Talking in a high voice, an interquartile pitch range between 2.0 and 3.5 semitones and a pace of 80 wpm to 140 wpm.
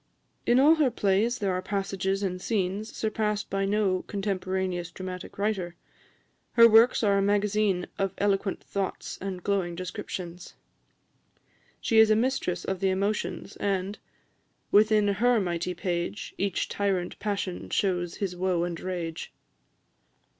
Yes: high, 195 Hz; narrow, 2.4 semitones; slow, 135 wpm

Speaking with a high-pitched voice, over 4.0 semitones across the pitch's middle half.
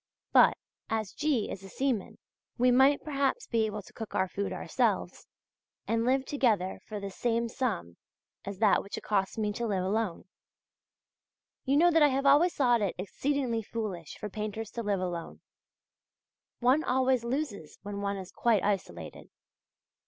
Yes: high, 225 Hz; average, 4.7 semitones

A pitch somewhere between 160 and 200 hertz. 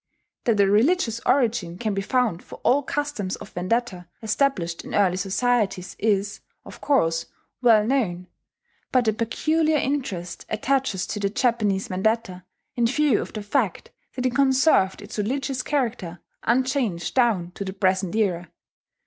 No: high, 220 Hz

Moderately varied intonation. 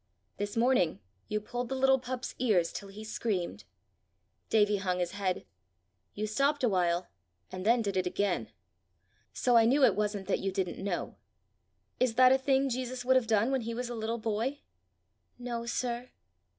Yes: average, 4.0 semitones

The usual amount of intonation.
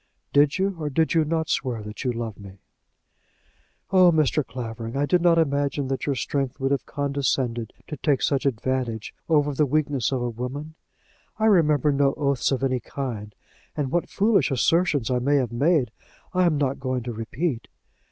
Yes: average, 3.6 semitones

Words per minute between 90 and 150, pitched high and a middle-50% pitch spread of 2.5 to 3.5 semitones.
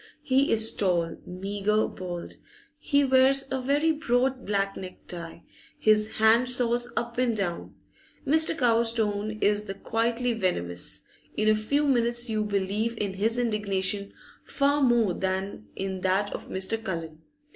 No: average, 145 wpm; high, 215 Hz; average, 4.1 semitones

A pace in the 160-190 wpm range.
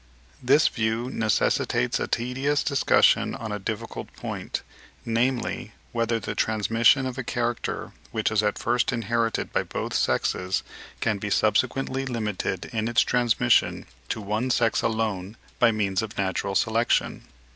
No: average, 140 wpm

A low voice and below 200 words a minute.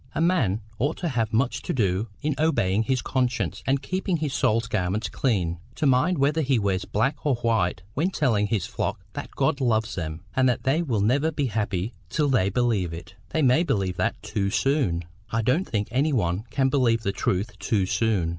No: low, 115 Hz; fast, 205 wpm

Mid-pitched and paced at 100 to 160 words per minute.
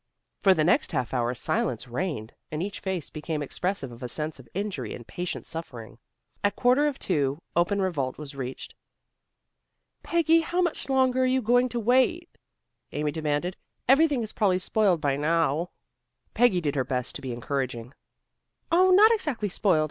No: medium, 175 Hz; average, 170 wpm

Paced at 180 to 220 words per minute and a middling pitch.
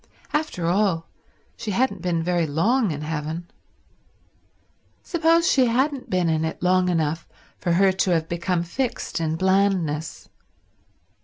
No: slow, 135 wpm; medium, 180 Hz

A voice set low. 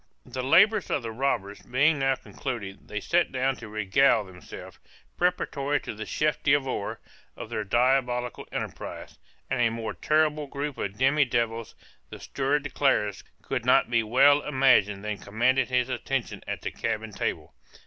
Yes: low, 130 Hz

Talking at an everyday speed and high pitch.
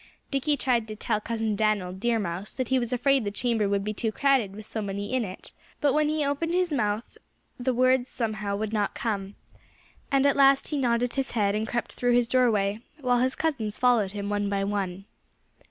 No: fast, 210 wpm; high, 230 Hz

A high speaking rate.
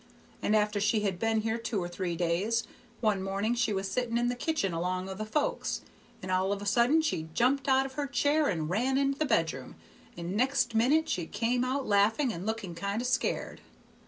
Yes: fast, 215 wpm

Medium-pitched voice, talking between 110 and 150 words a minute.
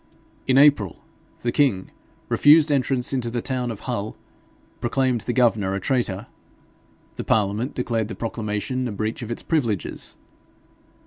No: low, 120 Hz; average, 140 wpm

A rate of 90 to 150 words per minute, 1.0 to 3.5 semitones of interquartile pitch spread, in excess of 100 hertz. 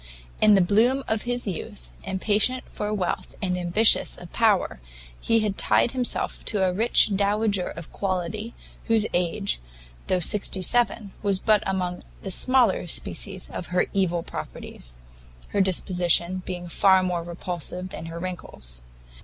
Yes: average, 145 wpm; average, 3.1 semitones; high, 190 Hz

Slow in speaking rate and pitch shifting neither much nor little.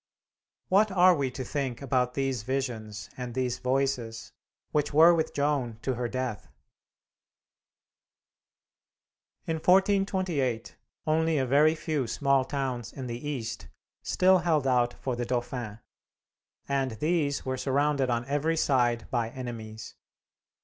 Yes: slow, 130 wpm; average, 3.6 semitones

